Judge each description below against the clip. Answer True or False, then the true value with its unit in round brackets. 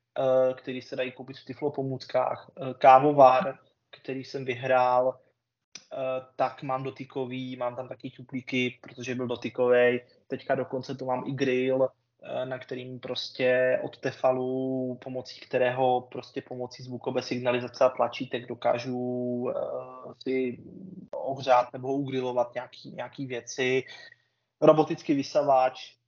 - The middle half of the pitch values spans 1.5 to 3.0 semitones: False (1.0 semitones)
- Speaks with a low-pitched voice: True (130 Hz)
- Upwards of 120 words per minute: False (115 wpm)